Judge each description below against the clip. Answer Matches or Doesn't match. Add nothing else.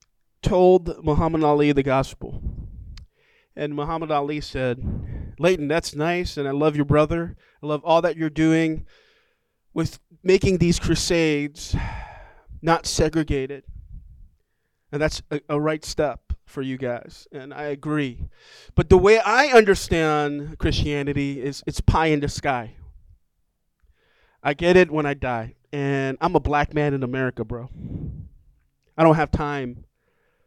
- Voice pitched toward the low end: Doesn't match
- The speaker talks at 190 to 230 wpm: Doesn't match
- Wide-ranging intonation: Doesn't match